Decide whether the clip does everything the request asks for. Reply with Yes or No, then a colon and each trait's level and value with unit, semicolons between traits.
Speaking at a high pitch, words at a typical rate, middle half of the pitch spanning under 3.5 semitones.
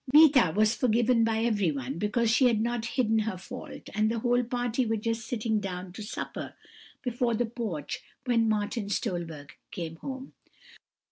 Yes: high, 225 Hz; average, 160 wpm; average, 2.8 semitones